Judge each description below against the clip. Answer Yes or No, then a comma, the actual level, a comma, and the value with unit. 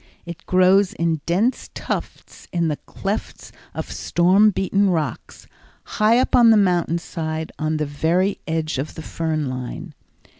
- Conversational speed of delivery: Yes, average, 150 wpm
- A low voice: No, medium, 170 Hz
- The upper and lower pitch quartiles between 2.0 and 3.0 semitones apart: No, average, 3.8 semitones